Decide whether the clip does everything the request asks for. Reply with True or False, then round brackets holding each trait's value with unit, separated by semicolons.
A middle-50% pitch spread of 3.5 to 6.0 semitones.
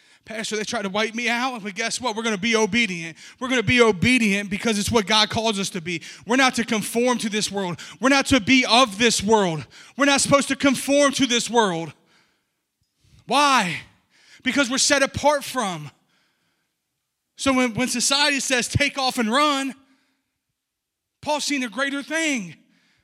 True (4.0 semitones)